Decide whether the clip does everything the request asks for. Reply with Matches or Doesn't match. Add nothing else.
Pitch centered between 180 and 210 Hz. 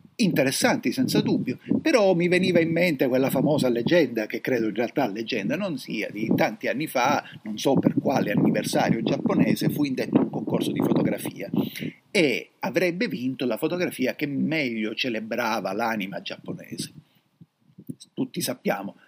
Doesn't match